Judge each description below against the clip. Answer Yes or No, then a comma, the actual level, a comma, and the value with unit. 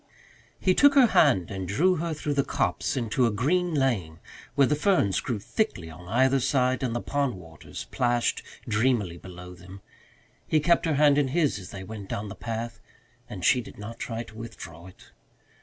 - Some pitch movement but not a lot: No, wide, 6.7 semitones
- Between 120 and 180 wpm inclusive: No, average, 190 wpm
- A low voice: Yes, low, 120 Hz